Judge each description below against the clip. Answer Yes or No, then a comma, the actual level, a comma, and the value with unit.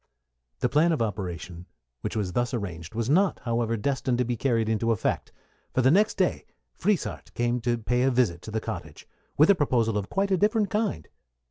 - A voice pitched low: Yes, low, 120 Hz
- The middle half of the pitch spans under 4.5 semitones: No, wide, 5.6 semitones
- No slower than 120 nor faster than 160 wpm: No, average, 200 wpm